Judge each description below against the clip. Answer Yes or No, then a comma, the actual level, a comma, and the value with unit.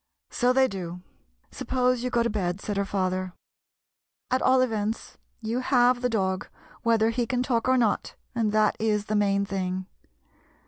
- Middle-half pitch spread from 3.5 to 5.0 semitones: Yes, average, 4.0 semitones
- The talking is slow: No, average, 175 wpm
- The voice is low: No, high, 220 Hz